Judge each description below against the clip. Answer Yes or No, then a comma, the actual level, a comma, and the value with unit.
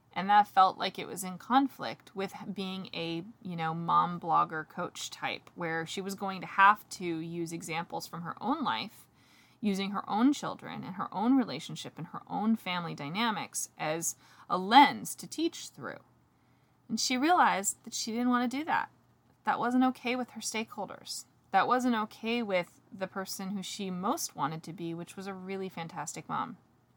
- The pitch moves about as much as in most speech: No, wide, 5.7 semitones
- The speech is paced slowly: No, average, 185 wpm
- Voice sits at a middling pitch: No, high, 195 Hz